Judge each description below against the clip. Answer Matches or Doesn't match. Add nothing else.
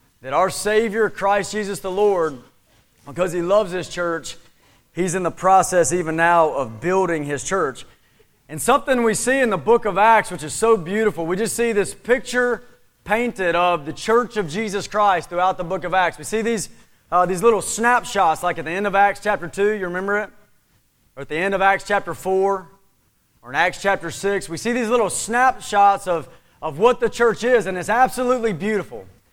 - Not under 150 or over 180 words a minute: Doesn't match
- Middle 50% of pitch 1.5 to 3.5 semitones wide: Doesn't match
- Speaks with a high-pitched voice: Matches